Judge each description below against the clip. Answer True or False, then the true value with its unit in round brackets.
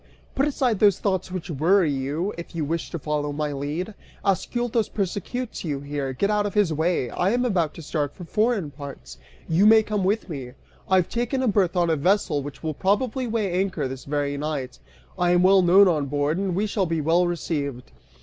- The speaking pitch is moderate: True (175 Hz)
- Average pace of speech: False (210 wpm)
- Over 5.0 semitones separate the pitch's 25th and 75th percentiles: True (5.5 semitones)